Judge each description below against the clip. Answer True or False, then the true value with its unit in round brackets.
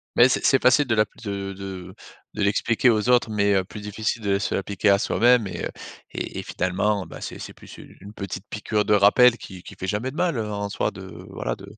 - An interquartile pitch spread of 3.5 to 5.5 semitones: False (2.5 semitones)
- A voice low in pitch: True (105 Hz)